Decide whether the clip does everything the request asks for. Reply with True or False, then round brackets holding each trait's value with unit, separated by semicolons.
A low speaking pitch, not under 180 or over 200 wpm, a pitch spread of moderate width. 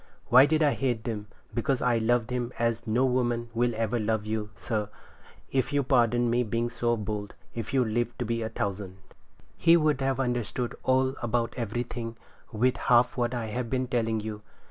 False (120 Hz; 190 wpm; 2.1 semitones)